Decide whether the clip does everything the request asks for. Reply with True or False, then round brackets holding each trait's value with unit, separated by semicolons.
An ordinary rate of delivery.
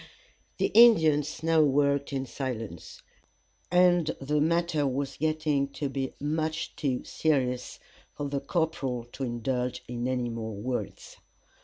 False (130 wpm)